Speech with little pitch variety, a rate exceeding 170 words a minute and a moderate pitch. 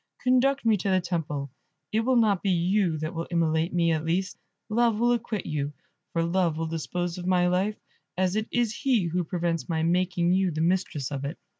No: average, 3.9 semitones; fast, 205 wpm; medium, 180 Hz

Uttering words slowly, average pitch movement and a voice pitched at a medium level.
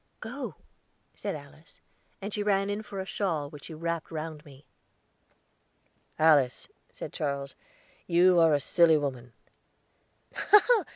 Yes: slow, 125 wpm; average, 4.0 semitones; medium, 160 Hz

